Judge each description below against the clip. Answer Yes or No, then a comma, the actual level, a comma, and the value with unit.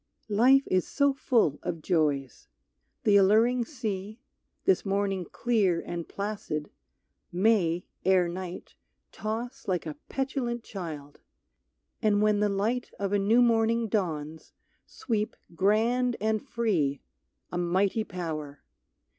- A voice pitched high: Yes, high, 205 Hz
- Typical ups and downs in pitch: Yes, average, 4.7 semitones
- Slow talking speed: Yes, slow, 120 wpm